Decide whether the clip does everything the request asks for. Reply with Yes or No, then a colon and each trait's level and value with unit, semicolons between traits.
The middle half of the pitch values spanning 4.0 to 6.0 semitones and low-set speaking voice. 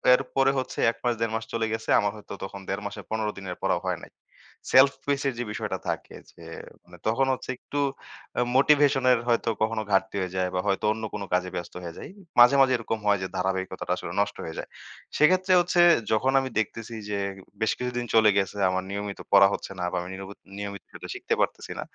Yes: average, 4.5 semitones; low, 110 Hz